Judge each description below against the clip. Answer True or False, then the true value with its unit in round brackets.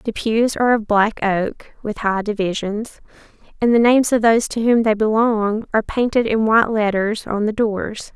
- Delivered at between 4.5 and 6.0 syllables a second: True (5.0 syllables/s)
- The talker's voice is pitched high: True (220 Hz)